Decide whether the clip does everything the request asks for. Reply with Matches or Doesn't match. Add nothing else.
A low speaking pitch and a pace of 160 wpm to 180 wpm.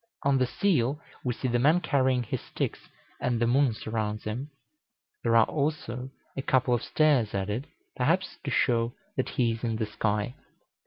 Matches